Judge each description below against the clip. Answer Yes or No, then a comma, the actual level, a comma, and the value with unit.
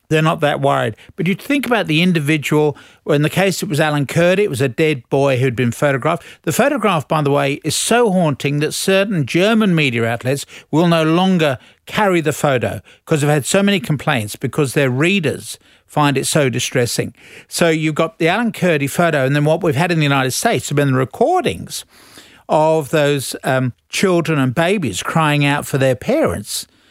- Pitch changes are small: No, average, 3.5 semitones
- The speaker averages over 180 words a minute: Yes, average, 200 wpm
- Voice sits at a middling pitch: Yes, medium, 150 Hz